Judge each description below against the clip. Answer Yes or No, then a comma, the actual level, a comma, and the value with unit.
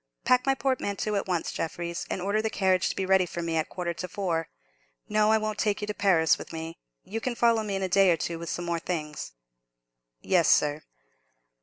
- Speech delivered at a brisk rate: Yes, fast, 225 wpm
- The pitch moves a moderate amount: Yes, average, 3.9 semitones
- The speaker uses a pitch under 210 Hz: Yes, medium, 185 Hz